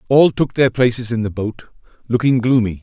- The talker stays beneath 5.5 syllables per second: No, 5.6 syllables/s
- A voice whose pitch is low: Yes, low, 120 Hz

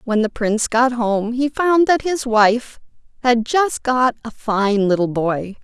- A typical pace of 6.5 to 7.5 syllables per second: No, 3.9 syllables/s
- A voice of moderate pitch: No, high, 235 Hz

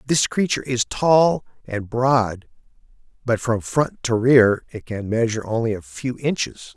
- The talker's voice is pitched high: No, low, 125 Hz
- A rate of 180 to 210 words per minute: No, average, 160 wpm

